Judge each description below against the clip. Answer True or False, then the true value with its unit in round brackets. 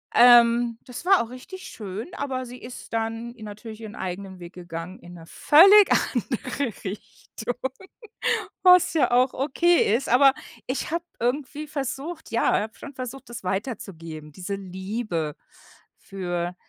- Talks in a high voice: True (235 Hz)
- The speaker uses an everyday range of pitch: False (6.0 semitones)